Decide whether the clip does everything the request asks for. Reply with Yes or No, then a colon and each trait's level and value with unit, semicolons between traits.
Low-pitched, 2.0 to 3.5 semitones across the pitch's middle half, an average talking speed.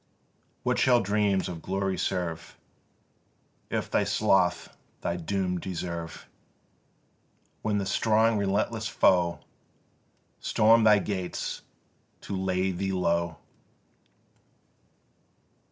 No: very low, 95 Hz; average, 2.7 semitones; slow, 90 wpm